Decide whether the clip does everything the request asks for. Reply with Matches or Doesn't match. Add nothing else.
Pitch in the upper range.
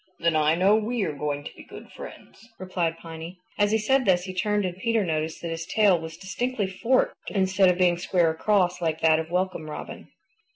Doesn't match